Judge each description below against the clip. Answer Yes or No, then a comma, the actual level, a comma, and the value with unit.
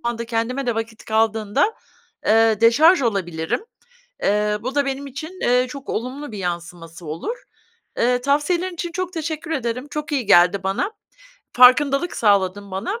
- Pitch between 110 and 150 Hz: No, high, 240 Hz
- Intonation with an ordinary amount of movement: No, wide, 5.9 semitones